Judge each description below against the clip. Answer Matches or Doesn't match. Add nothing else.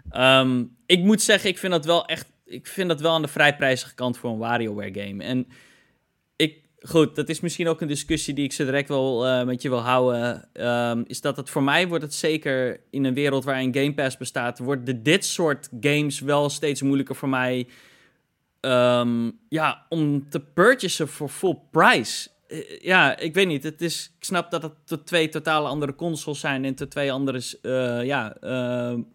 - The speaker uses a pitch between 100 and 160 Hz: Matches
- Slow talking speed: Doesn't match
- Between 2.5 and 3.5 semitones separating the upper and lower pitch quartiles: Doesn't match